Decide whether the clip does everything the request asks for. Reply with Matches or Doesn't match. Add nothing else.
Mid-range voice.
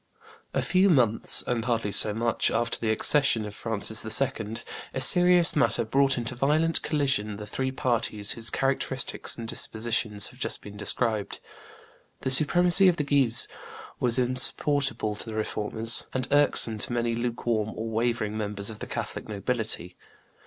Doesn't match